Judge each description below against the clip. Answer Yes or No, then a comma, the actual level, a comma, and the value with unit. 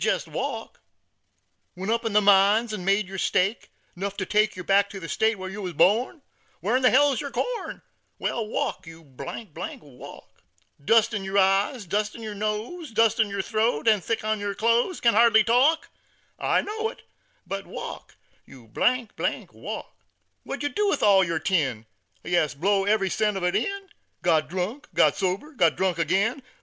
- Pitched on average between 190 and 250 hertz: Yes, high, 205 Hz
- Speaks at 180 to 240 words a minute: Yes, average, 185 wpm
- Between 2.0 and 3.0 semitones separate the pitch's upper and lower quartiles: No, average, 3.6 semitones